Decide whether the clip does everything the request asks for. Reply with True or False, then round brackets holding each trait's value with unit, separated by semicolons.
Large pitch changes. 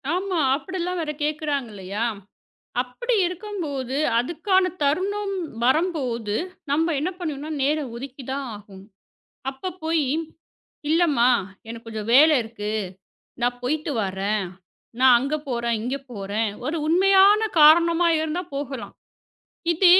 True (6.3 semitones)